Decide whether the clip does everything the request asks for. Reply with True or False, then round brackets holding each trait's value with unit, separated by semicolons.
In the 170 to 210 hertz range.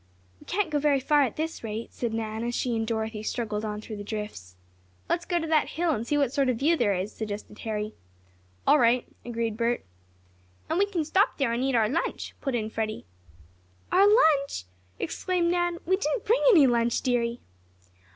False (245 Hz)